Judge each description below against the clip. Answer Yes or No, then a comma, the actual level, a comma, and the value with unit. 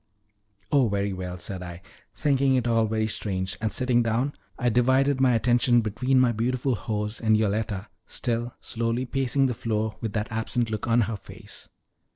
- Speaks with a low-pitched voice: Yes, low, 115 Hz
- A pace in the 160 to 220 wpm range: Yes, average, 175 wpm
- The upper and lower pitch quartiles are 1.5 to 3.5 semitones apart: Yes, average, 2.9 semitones